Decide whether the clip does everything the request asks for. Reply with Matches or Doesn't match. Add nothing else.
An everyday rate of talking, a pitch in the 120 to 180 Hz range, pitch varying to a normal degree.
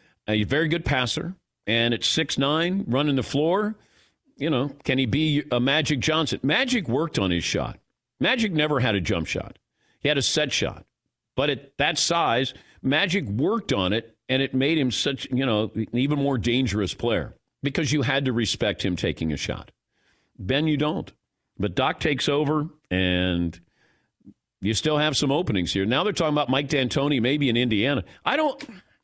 Matches